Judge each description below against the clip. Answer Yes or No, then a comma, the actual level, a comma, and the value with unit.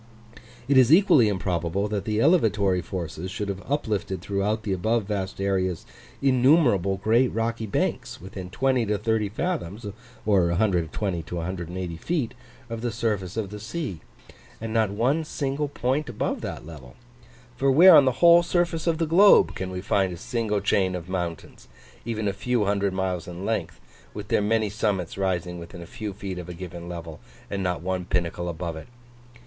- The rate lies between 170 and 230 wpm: Yes, average, 175 wpm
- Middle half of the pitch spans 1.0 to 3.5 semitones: No, average, 4.4 semitones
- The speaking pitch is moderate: No, low, 100 Hz